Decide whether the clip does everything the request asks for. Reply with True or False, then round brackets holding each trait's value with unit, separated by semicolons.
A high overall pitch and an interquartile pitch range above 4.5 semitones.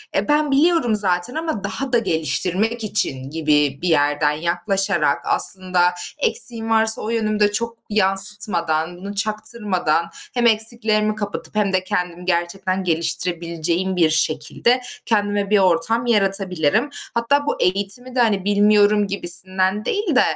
False (200 Hz; 4.1 semitones)